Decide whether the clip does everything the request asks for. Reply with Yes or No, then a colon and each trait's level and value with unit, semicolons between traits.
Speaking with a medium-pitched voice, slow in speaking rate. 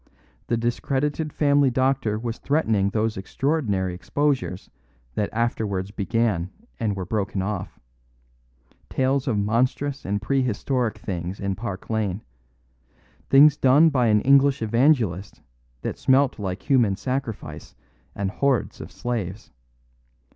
No: low, 115 Hz; slow, 120 wpm